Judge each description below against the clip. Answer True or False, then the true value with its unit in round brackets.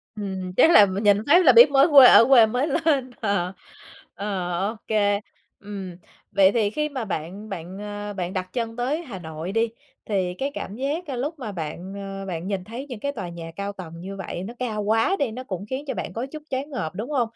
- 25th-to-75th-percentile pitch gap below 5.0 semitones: False (5.3 semitones)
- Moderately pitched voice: False (210 Hz)